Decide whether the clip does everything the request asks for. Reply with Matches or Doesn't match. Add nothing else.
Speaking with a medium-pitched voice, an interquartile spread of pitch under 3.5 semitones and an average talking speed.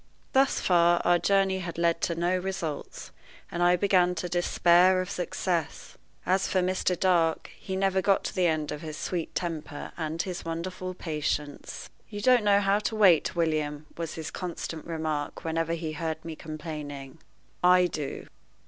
Matches